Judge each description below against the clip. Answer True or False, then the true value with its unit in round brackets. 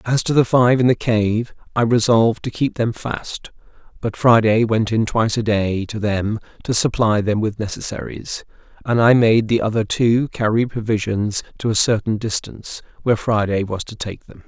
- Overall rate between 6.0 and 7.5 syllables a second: False (4.9 syllables/s)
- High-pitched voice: False (110 Hz)